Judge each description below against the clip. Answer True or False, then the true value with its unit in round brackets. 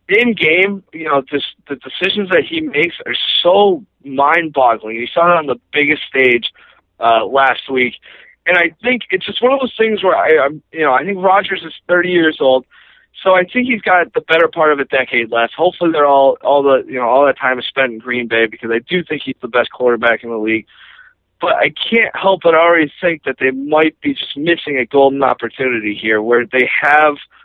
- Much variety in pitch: True (6.0 semitones)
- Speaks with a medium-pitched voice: True (150 Hz)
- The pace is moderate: False (225 wpm)